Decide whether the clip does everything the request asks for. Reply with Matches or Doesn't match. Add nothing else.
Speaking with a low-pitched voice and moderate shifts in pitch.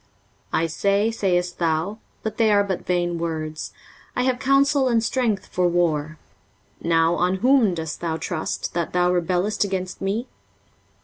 Doesn't match